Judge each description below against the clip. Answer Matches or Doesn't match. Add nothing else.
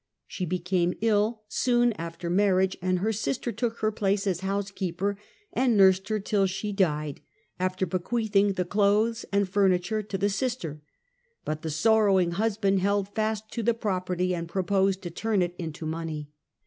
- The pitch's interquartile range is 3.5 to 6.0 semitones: Doesn't match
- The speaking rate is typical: Matches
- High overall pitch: Matches